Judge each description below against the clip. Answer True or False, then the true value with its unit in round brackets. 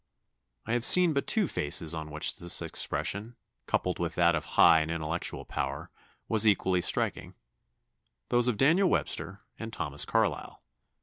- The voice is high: False (90 Hz)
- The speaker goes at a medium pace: True (150 wpm)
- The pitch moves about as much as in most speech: False (7.0 semitones)